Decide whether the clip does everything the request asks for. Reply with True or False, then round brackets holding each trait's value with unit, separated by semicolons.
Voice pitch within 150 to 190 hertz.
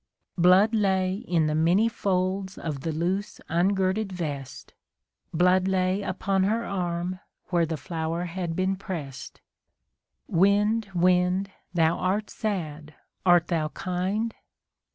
True (185 Hz)